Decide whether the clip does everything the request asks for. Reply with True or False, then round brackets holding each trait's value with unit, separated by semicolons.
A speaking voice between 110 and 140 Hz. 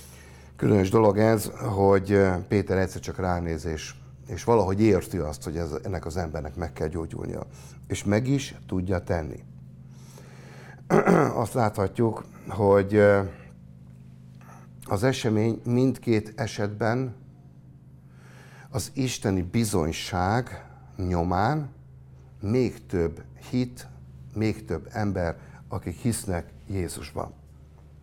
False (95 Hz)